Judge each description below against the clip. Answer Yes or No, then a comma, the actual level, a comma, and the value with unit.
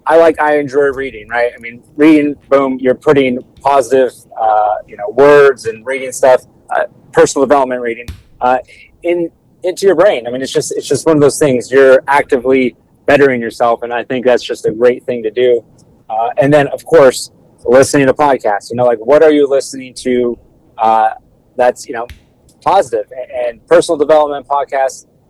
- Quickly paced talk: No, average, 185 wpm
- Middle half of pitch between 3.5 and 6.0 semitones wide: Yes, average, 3.8 semitones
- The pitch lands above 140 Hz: No, low, 135 Hz